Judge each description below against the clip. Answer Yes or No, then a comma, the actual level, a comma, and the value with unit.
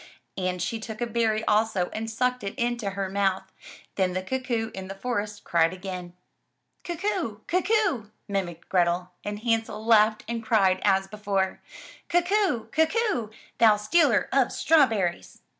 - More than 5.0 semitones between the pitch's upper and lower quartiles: No, average, 4.0 semitones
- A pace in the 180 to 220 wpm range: No, average, 160 wpm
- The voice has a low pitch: No, high, 215 Hz